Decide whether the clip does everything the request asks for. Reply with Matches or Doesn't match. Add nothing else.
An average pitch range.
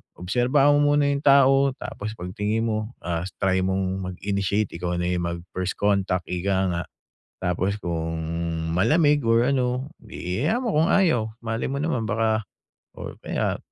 Doesn't match